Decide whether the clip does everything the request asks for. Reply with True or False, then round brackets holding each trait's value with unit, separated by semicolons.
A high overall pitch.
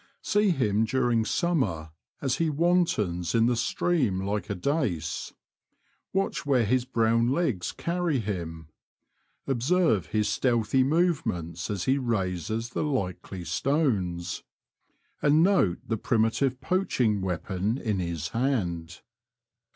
False (115 Hz)